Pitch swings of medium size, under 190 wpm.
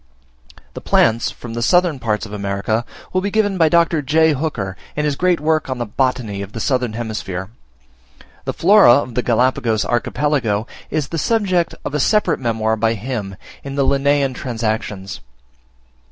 No: wide, 5.7 semitones; average, 170 wpm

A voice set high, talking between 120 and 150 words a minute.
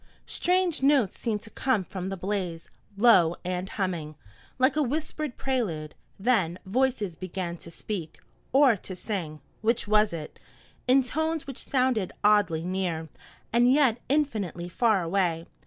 Yes: high, 205 Hz; average, 140 wpm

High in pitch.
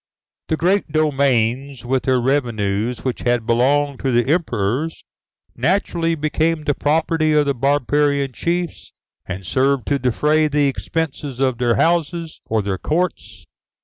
No: medium, 140 Hz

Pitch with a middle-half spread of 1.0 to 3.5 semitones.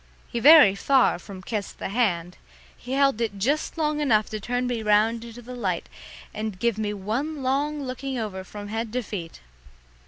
No: average, 4.1 semitones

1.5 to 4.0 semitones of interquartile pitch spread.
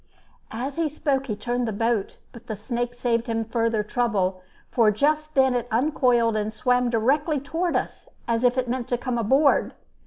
Yes: average, 2.8 semitones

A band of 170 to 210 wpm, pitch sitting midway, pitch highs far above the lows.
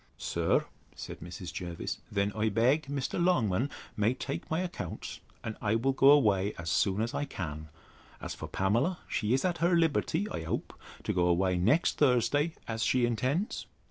No: average, 175 wpm; low, 115 Hz; wide, 7.1 semitones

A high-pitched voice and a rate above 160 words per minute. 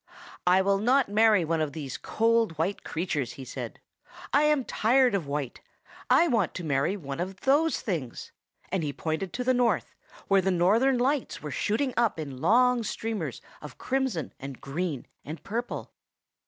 Yes: high, 195 Hz; average, 170 wpm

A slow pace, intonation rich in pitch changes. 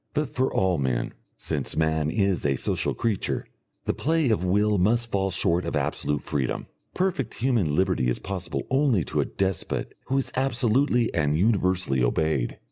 No: average, 165 wpm; wide, 7.1 semitones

